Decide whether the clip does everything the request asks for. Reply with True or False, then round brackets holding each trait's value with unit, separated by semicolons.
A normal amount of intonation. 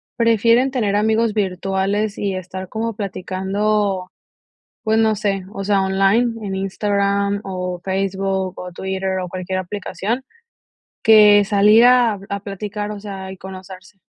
False (1.9 semitones)